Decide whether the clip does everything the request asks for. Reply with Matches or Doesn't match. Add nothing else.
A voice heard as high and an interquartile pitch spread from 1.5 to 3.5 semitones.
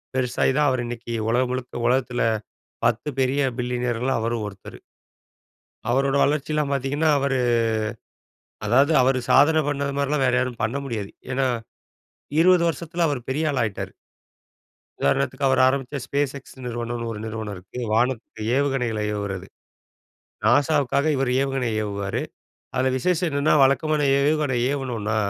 Doesn't match